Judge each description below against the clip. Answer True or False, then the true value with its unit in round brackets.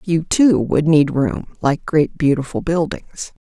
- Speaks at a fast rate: False (140 wpm)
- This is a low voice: False (160 Hz)